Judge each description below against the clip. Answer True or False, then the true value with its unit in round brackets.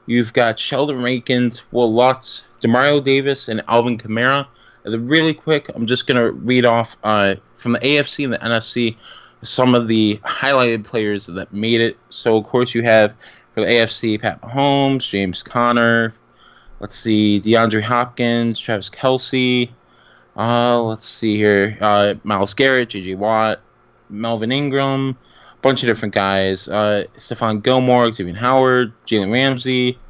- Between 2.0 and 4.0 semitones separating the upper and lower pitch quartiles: True (2.7 semitones)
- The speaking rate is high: False (150 wpm)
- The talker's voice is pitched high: False (115 Hz)